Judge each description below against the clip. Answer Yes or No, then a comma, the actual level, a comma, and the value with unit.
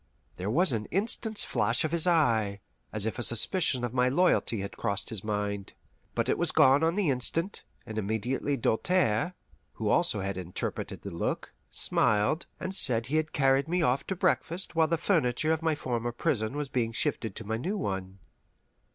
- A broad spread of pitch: Yes, wide, 7.0 semitones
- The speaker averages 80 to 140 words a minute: No, average, 185 wpm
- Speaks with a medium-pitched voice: No, low, 125 Hz